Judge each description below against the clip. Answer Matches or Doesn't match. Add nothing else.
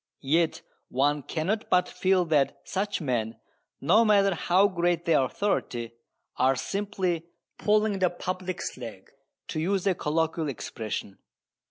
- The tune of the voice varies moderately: Doesn't match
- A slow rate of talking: Matches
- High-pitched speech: Doesn't match